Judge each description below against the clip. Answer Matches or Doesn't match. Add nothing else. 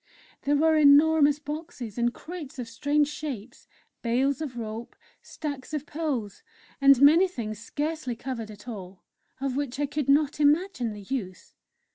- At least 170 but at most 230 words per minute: Doesn't match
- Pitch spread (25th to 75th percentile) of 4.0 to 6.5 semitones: Matches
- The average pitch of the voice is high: Matches